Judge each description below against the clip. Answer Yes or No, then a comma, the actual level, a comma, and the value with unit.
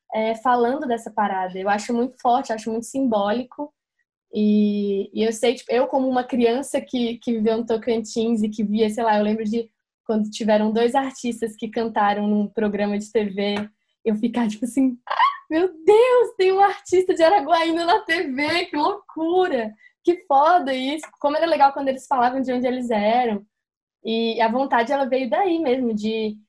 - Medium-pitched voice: No, high, 240 Hz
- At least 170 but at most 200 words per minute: Yes, average, 180 wpm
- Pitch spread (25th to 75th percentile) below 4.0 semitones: No, average, 4.5 semitones